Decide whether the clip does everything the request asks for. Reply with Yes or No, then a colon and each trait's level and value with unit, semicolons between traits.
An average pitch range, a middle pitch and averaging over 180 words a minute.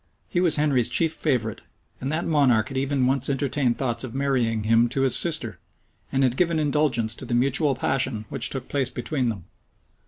No: average, 3.2 semitones; low, 130 Hz; average, 190 wpm